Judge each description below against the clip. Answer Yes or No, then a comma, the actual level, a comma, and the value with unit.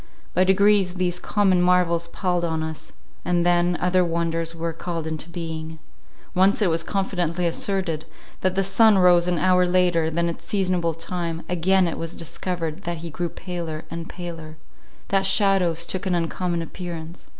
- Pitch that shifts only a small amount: Yes, narrow, 1.8 semitones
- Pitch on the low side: No, medium, 175 Hz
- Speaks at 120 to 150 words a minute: No, average, 165 wpm